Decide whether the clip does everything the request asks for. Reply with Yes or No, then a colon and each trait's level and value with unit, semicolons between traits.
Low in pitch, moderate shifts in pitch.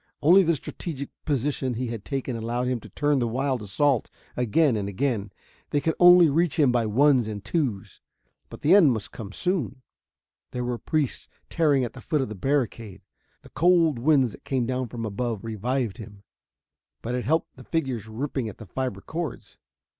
Yes: low, 130 Hz; average, 4.5 semitones